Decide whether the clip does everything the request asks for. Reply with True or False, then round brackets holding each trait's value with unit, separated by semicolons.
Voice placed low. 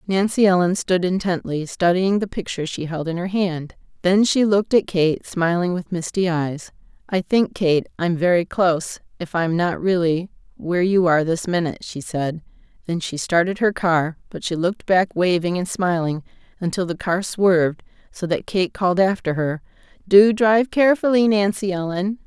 False (180 Hz)